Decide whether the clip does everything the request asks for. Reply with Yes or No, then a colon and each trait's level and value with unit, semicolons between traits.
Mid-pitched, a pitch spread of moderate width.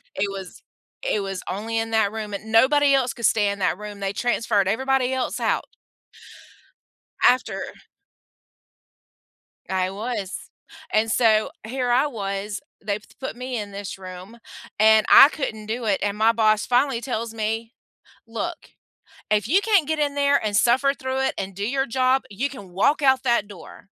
No: high, 225 Hz; average, 4.3 semitones